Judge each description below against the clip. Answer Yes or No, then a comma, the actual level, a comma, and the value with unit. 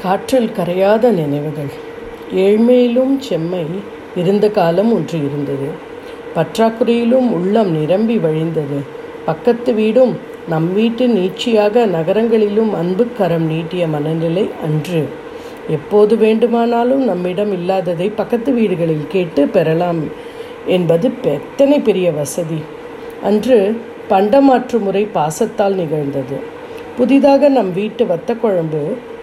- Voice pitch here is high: Yes, high, 205 Hz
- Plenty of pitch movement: Yes, wide, 6.3 semitones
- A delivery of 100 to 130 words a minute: No, average, 90 wpm